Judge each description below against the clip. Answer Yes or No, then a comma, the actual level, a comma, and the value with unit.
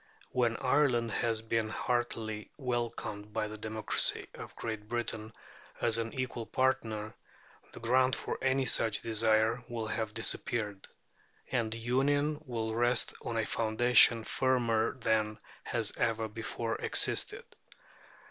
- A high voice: No, low, 115 Hz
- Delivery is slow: Yes, slow, 125 wpm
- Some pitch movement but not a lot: No, narrow, 1.9 semitones